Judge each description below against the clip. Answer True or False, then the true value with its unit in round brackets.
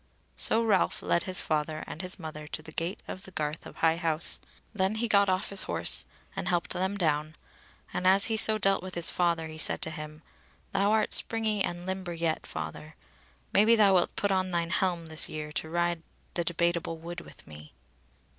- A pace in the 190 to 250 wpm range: True (200 wpm)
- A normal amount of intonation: True (3.2 semitones)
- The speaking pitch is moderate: True (175 Hz)